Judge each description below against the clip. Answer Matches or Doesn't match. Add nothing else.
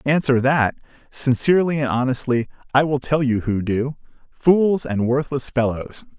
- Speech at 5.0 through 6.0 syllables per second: Doesn't match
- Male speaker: Matches